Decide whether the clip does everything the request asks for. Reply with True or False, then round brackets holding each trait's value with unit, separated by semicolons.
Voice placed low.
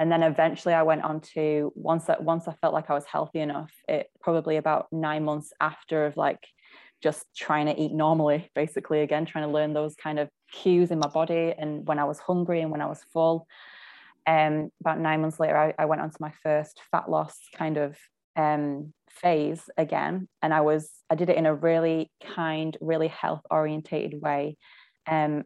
False (155 Hz)